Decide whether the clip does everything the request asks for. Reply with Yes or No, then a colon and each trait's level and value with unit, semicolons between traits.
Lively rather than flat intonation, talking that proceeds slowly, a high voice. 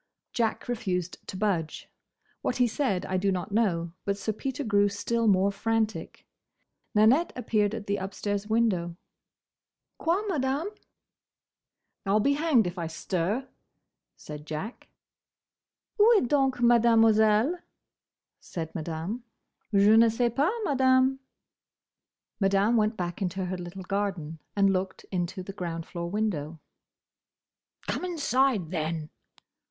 No: average, 4.7 semitones; slow, 125 wpm; high, 205 Hz